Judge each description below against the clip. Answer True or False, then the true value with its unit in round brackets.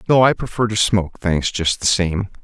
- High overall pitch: False (100 Hz)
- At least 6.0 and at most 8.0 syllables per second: False (5.3 syllables/s)